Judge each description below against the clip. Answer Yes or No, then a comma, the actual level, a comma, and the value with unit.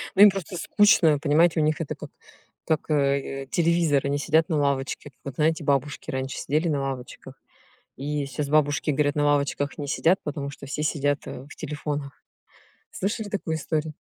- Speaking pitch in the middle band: Yes, medium, 150 Hz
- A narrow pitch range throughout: Yes, narrow, 2.2 semitones